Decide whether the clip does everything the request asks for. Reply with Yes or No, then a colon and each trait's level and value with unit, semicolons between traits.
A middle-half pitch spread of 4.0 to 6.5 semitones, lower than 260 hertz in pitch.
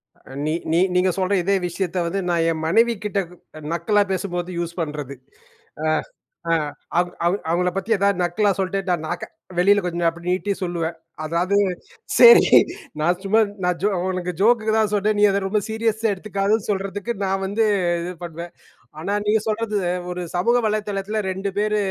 No: average, 3.1 semitones; high, 195 Hz